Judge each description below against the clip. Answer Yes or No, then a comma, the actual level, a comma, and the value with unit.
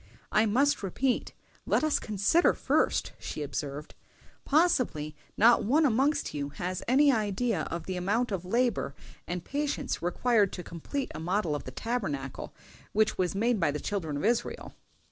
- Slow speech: No, average, 160 wpm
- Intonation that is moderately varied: No, wide, 6.8 semitones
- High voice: Yes, high, 205 Hz